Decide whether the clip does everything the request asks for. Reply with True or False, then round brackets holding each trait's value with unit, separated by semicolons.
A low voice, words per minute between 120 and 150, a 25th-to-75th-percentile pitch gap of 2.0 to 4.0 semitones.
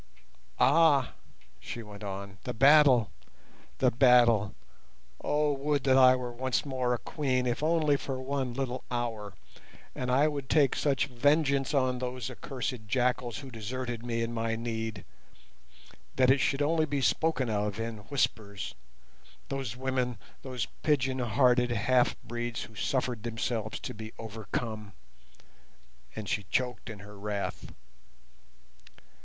True (125 Hz; 140 wpm; 3.1 semitones)